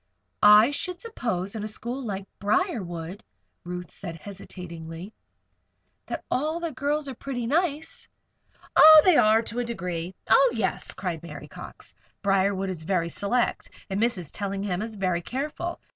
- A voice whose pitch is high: Yes, high, 210 Hz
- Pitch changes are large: Yes, wide, 6.5 semitones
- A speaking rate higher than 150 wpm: No, average, 145 wpm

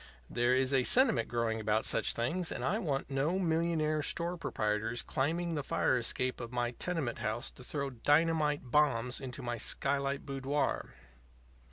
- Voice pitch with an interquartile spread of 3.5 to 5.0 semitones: Yes, average, 4.6 semitones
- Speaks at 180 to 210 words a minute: No, average, 160 wpm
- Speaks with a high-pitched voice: No, low, 135 Hz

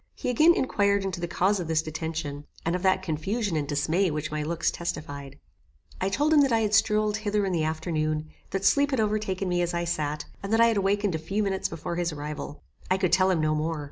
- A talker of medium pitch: Yes, medium, 180 Hz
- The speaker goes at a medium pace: No, fast, 235 wpm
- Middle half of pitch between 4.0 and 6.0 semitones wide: Yes, average, 4.7 semitones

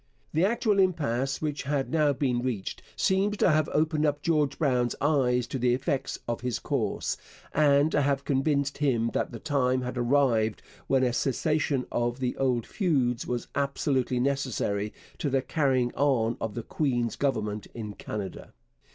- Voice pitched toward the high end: No, low, 135 Hz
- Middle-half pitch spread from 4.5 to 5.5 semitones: No, average, 3.3 semitones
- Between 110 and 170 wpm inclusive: Yes, average, 160 wpm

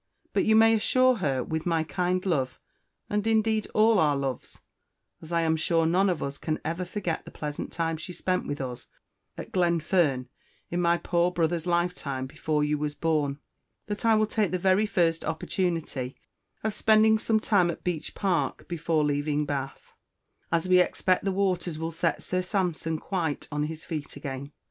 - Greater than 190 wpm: No, average, 180 wpm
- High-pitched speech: No, medium, 170 Hz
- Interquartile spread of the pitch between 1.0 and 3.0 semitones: No, average, 3.7 semitones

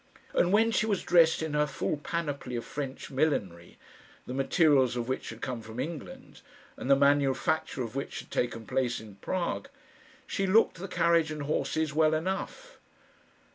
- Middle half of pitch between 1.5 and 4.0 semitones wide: No, average, 4.6 semitones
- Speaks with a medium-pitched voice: Yes, medium, 145 Hz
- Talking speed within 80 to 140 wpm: No, average, 170 wpm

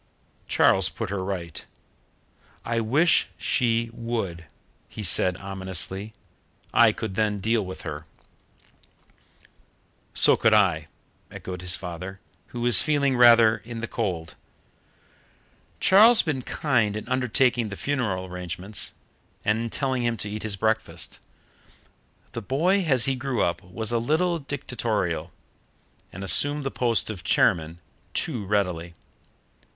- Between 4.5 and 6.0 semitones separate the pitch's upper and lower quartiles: Yes, average, 4.9 semitones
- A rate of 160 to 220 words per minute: No, slow, 135 wpm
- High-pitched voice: No, low, 110 Hz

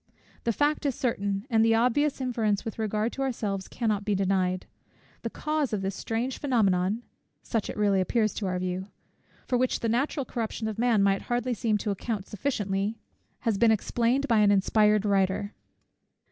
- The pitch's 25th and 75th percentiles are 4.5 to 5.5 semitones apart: No, average, 3.4 semitones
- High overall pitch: Yes, high, 220 Hz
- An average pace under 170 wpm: No, average, 175 wpm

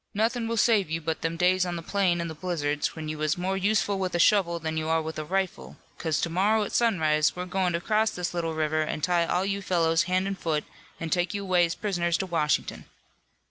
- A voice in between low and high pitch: Yes, medium, 175 Hz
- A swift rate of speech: Yes, fast, 245 wpm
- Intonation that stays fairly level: No, average, 3.1 semitones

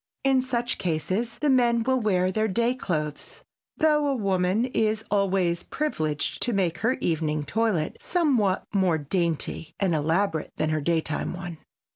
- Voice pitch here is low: No, high, 190 Hz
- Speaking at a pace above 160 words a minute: No, average, 150 wpm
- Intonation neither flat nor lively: No, wide, 6.3 semitones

